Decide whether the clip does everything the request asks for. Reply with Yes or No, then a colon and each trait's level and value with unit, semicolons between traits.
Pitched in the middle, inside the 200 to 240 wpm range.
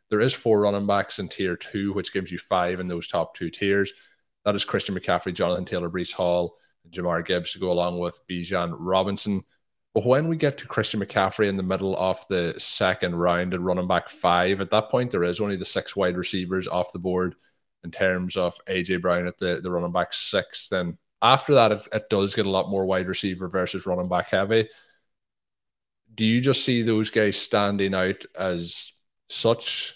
No: very low, 95 Hz; fast, 205 wpm